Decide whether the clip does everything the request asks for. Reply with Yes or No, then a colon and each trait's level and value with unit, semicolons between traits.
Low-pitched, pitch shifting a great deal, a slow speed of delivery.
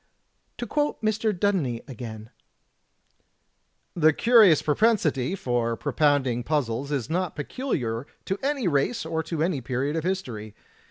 No: medium, 150 Hz; wide, 7.5 semitones; slow, 125 wpm